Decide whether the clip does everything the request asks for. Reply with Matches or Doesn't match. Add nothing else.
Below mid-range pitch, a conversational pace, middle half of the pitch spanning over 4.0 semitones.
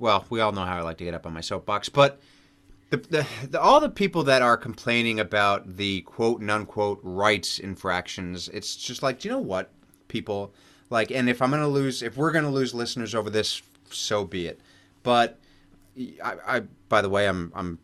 Doesn't match